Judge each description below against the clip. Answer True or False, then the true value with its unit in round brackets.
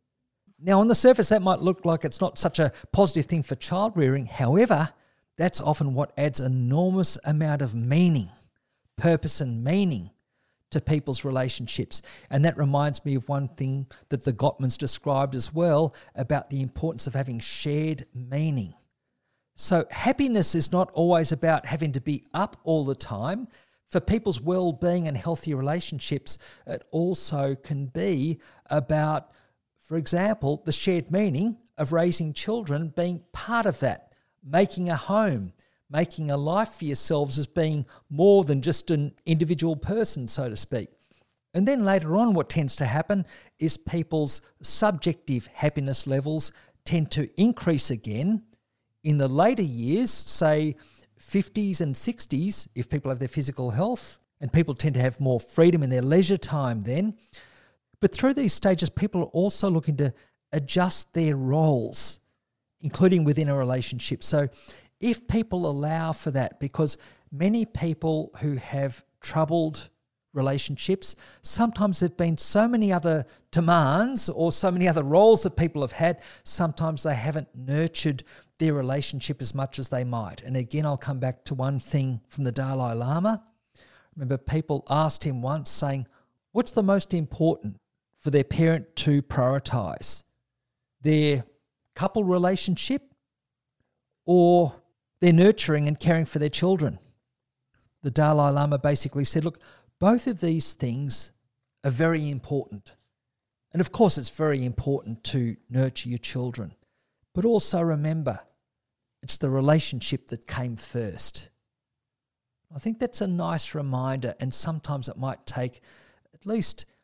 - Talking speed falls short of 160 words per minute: True (150 wpm)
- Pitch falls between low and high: True (150 Hz)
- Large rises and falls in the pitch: False (4.6 semitones)